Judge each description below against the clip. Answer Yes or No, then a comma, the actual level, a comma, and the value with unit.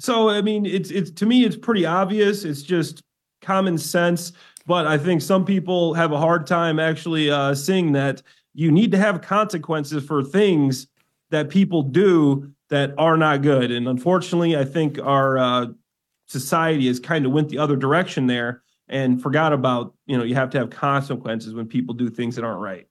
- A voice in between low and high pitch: Yes, medium, 155 Hz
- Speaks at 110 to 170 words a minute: No, average, 190 wpm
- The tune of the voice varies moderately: Yes, average, 4.6 semitones